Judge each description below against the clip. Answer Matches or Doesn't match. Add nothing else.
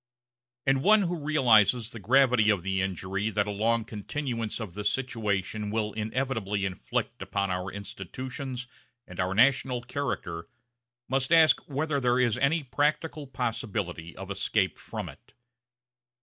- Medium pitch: Doesn't match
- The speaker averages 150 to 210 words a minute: Doesn't match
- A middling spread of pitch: Matches